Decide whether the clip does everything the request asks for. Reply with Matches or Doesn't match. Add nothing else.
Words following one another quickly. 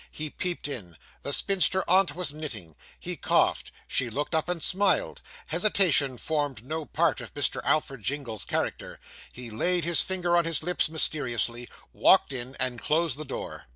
Doesn't match